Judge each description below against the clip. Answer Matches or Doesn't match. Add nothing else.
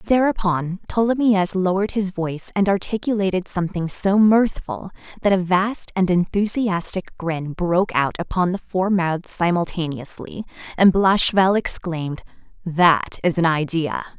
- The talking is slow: Matches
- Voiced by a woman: Matches